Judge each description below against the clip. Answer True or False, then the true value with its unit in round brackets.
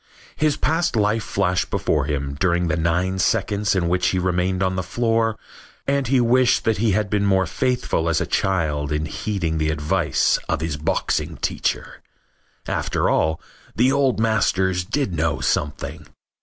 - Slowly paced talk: False (165 wpm)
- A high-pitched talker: False (95 Hz)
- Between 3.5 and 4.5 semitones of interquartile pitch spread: False (5.4 semitones)